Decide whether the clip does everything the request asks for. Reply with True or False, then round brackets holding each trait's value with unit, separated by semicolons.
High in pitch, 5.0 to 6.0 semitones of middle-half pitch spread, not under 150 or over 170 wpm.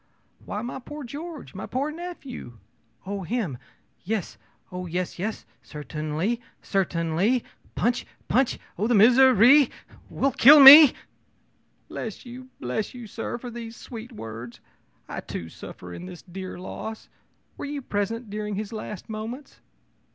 False (220 Hz; 5.5 semitones; 135 wpm)